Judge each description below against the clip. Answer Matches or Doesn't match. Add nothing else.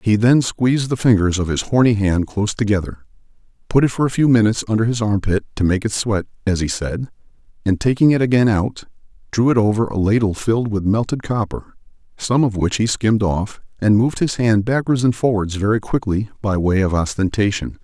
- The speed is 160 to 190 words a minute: Doesn't match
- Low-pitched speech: Matches